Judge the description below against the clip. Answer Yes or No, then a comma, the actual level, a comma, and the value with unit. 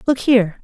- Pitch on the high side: Yes, high, 230 Hz